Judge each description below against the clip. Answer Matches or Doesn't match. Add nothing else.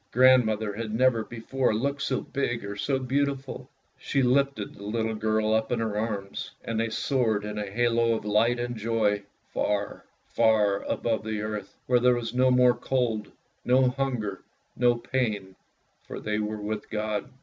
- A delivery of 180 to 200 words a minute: Doesn't match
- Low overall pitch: Matches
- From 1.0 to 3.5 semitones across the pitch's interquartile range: Matches